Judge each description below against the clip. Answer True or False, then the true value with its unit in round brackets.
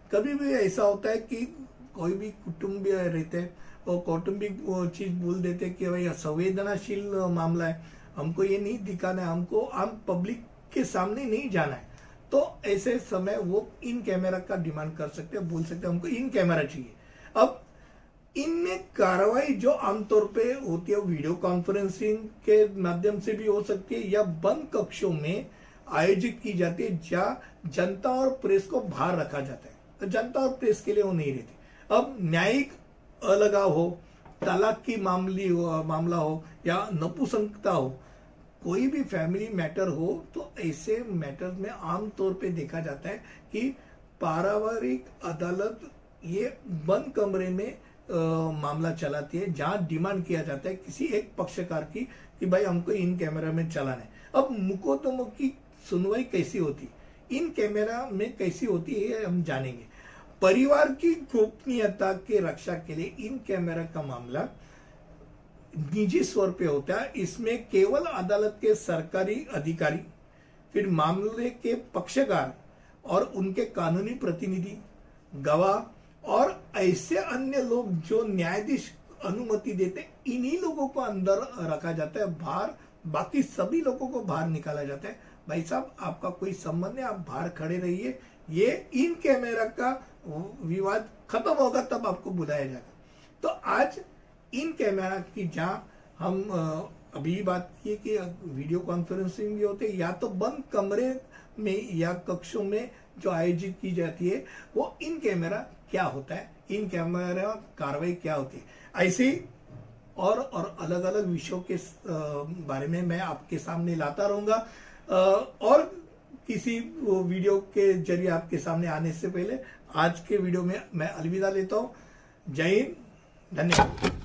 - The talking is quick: False (155 wpm)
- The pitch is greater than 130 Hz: True (190 Hz)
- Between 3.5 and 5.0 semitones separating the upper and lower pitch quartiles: True (4.3 semitones)